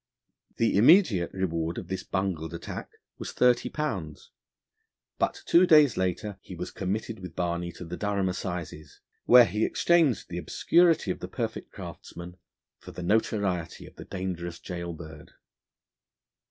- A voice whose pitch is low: Yes, very low, 95 Hz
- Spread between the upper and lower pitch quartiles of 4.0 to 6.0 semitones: Yes, average, 4.3 semitones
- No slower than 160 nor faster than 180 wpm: No, average, 145 wpm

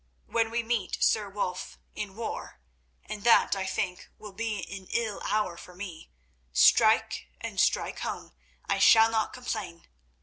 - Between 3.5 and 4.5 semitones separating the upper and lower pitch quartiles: Yes, average, 4.2 semitones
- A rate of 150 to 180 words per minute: No, average, 140 wpm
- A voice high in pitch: Yes, high, 200 Hz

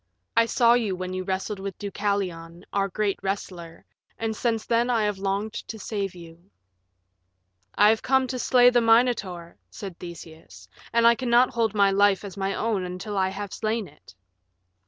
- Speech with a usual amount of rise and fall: Yes, average, 3.5 semitones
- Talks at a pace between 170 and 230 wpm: Yes, average, 175 wpm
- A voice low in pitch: No, high, 200 Hz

